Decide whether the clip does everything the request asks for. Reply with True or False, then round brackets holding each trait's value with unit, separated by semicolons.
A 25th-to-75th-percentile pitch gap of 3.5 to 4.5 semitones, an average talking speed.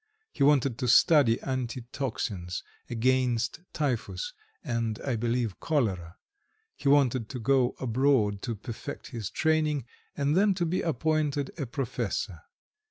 False (3.9 semitones; 130 wpm)